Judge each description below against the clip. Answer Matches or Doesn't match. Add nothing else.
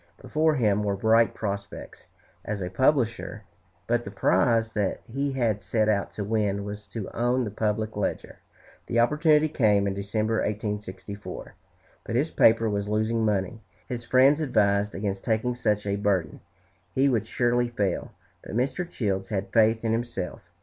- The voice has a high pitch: Doesn't match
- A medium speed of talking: Matches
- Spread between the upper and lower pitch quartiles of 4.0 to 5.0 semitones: Doesn't match